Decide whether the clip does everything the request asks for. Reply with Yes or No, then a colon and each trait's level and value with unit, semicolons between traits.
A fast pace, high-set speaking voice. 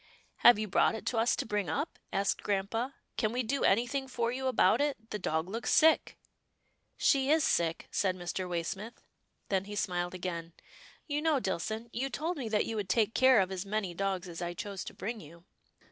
Yes: fast, 220 wpm; high, 210 Hz